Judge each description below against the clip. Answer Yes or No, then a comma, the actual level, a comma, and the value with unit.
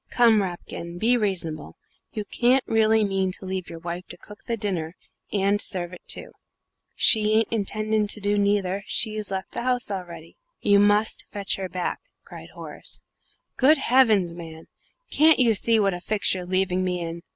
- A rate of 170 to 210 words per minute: Yes, average, 175 wpm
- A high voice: Yes, high, 200 Hz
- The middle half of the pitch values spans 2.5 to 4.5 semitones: Yes, average, 3.2 semitones